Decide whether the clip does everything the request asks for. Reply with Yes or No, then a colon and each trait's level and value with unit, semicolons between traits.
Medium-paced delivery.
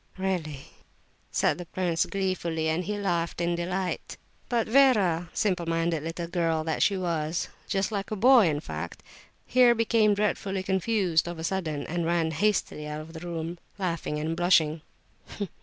Yes: average, 160 wpm